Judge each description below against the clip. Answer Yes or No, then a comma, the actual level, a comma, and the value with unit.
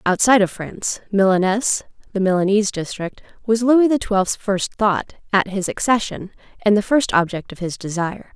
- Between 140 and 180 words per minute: Yes, average, 165 wpm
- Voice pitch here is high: Yes, high, 205 Hz